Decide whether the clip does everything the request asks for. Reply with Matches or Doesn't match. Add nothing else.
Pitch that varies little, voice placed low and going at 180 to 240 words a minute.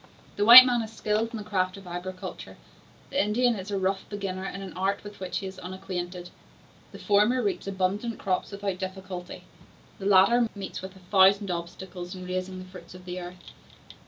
Doesn't match